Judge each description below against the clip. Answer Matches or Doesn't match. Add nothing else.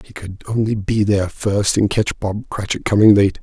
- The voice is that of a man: Matches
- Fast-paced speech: Matches